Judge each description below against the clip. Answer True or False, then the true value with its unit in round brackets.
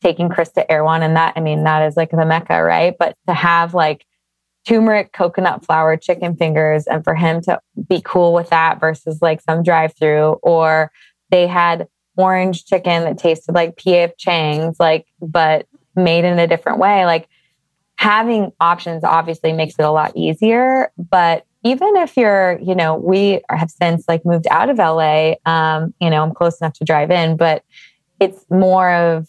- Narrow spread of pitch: True (2.1 semitones)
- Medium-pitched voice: True (170 Hz)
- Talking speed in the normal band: True (180 wpm)